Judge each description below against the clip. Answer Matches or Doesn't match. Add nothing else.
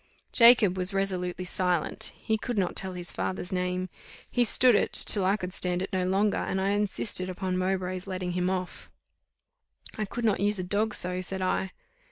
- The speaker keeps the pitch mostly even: Matches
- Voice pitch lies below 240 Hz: Matches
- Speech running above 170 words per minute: Matches